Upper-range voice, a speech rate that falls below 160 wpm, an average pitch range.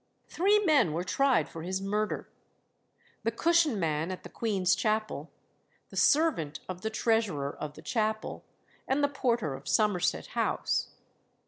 No: high, 215 Hz; average, 145 wpm; wide, 6.8 semitones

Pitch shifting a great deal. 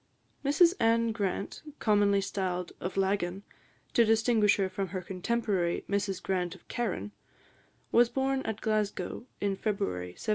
No: average, 3.3 semitones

